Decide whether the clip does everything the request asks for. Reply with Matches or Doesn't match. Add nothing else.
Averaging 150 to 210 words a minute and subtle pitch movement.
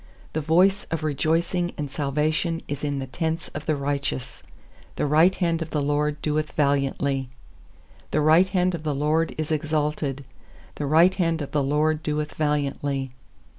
Matches